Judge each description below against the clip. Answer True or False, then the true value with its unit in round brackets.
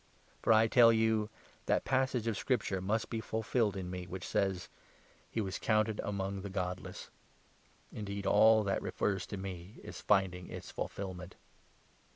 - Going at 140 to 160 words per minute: False (175 wpm)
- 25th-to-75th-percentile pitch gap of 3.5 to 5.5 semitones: False (2.8 semitones)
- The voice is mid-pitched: False (100 Hz)